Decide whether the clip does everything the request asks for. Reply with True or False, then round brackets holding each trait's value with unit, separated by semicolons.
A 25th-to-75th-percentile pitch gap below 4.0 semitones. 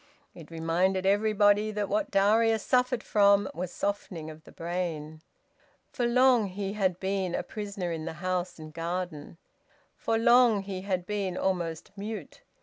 True (3.2 semitones)